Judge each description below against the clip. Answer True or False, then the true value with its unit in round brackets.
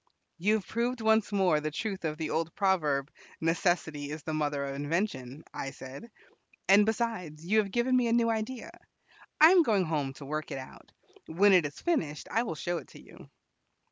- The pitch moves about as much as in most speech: False (6.5 semitones)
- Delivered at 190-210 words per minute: True (200 wpm)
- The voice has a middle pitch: True (175 Hz)